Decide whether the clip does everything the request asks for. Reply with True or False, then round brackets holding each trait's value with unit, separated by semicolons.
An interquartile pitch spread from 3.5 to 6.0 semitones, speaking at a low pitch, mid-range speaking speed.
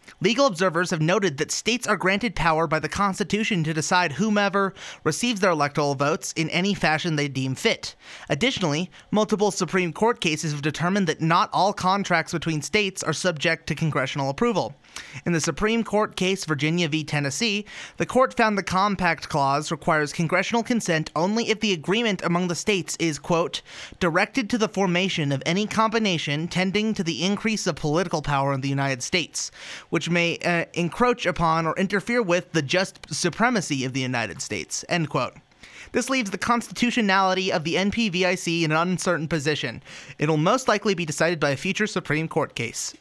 False (4.3 semitones; 175 Hz; 175 wpm)